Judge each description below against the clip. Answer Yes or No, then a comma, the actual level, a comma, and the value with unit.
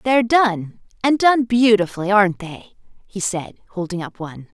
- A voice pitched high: Yes, high, 205 Hz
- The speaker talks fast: No, average, 155 wpm